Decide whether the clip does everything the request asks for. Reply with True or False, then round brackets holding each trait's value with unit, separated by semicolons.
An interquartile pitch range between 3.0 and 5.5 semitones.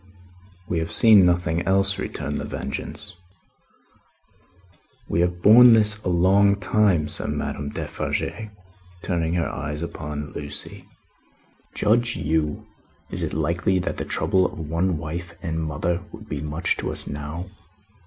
True (3.9 semitones)